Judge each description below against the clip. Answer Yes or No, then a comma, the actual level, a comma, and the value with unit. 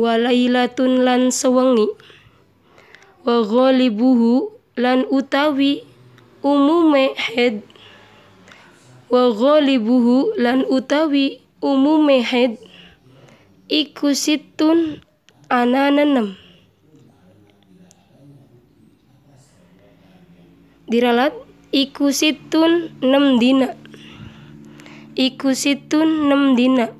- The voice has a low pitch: No, very high, 250 Hz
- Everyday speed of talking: No, slow, 55 wpm